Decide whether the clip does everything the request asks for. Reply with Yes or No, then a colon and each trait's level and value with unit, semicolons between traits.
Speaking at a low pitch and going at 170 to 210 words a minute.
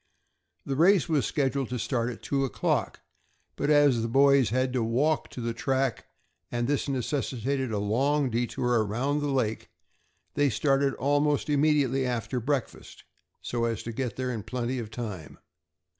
No: low, 130 Hz; average, 160 wpm